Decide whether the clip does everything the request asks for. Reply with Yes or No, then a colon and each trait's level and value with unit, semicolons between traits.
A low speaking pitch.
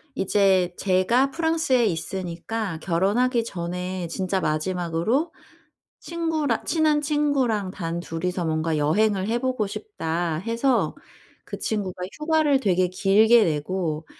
No: high, 195 Hz